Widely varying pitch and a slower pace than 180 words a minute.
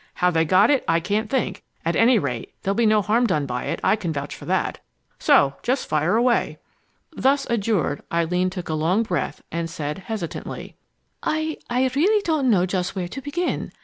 No: wide, 6.6 semitones; average, 195 wpm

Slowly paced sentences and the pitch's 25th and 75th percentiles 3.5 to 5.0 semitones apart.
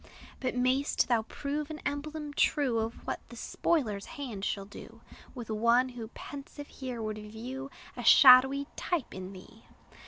No: average, 155 wpm; average, 4.3 semitones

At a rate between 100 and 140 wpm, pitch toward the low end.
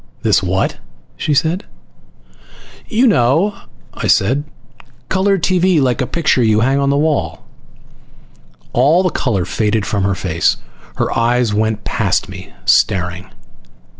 Yes: slow, 135 wpm; low, 125 Hz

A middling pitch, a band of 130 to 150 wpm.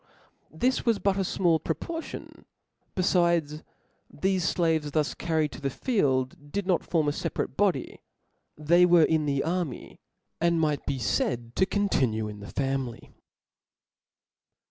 Yes: medium, 160 Hz; average, 145 wpm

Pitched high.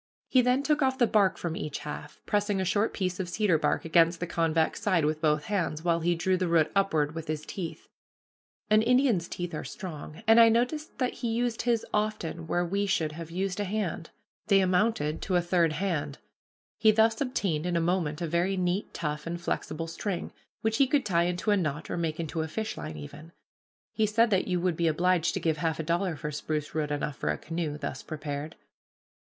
No: medium, 175 Hz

